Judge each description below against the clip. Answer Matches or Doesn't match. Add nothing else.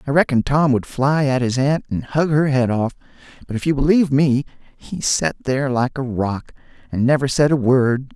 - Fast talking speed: Matches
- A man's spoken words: Matches